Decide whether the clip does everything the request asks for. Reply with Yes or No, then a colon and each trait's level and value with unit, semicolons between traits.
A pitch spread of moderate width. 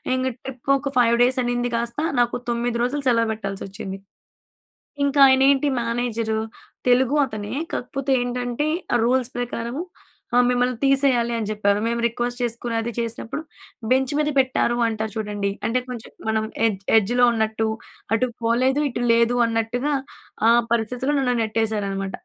No: narrow, 2.2 semitones